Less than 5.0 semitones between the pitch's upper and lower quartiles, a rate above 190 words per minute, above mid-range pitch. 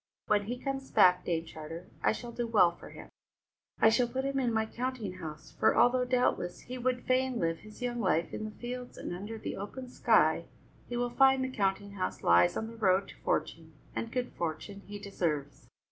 No: wide, 5.5 semitones; fast, 205 wpm; high, 220 Hz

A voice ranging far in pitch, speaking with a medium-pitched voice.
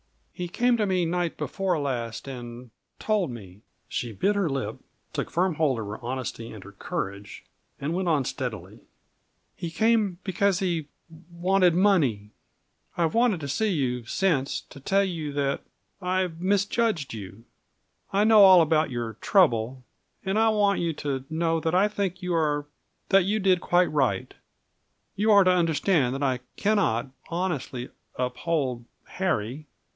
Yes: wide, 6.8 semitones; medium, 165 Hz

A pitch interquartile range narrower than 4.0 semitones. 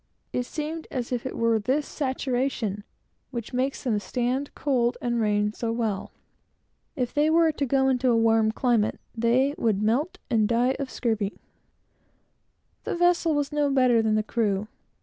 Yes: average, 3.5 semitones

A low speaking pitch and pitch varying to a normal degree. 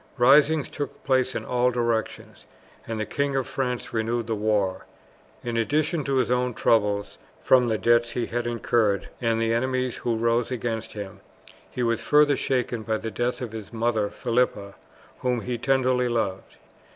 No: low, 120 Hz; narrow, 2.1 semitones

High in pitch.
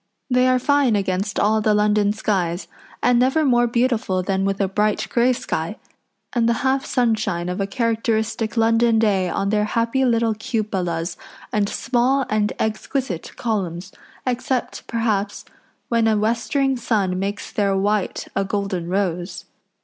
Yes: high, 215 Hz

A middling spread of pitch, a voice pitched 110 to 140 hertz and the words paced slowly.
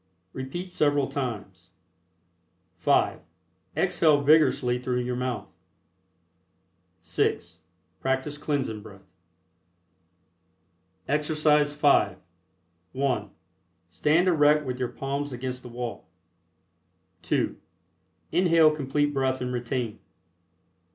Yes: average, 3.1 semitones; low, 135 Hz; slow, 85 wpm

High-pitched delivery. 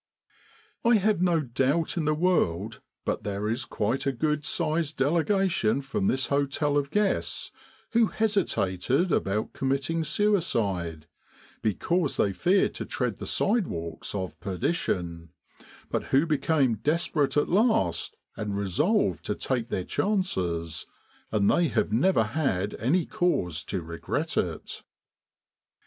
No: medium, 140 Hz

